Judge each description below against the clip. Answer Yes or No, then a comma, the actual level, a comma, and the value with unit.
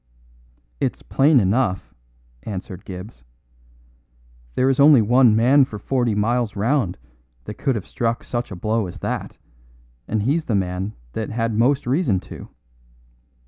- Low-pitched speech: Yes, low, 115 Hz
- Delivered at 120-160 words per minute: Yes, average, 145 wpm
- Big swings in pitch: No, average, 4.3 semitones